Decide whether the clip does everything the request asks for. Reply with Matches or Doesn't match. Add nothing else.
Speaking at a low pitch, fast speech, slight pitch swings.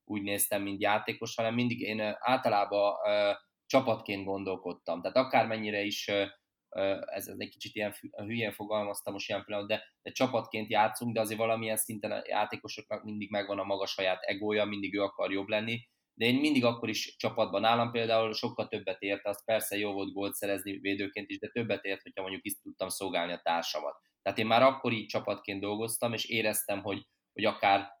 Matches